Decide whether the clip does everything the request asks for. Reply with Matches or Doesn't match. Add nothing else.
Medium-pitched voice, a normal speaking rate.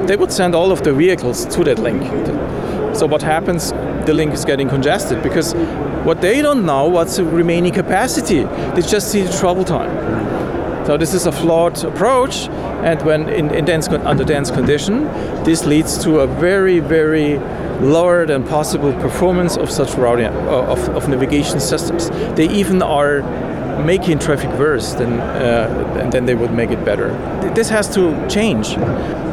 Matches